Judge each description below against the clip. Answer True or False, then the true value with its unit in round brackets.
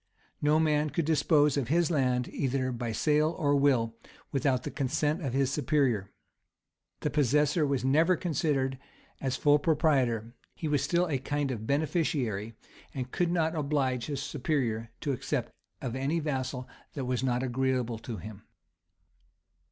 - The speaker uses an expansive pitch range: False (3.2 semitones)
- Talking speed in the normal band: True (155 wpm)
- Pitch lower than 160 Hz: True (140 Hz)